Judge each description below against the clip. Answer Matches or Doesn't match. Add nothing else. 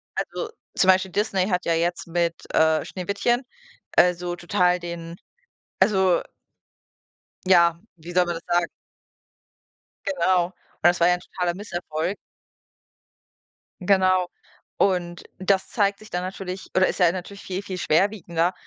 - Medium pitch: Matches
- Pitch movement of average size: Doesn't match